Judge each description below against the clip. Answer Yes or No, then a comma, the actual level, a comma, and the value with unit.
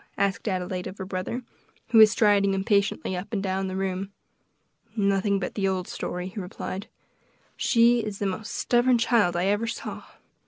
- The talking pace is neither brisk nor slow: Yes, average, 170 wpm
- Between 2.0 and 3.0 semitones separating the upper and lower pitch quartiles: Yes, narrow, 2.5 semitones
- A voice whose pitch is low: No, high, 195 Hz